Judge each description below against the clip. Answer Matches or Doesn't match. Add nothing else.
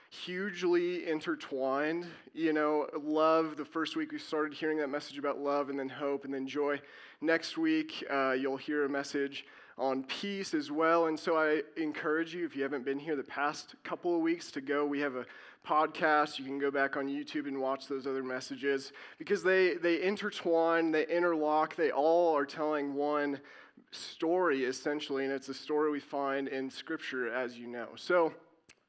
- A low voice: Doesn't match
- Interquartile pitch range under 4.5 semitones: Matches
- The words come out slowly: Doesn't match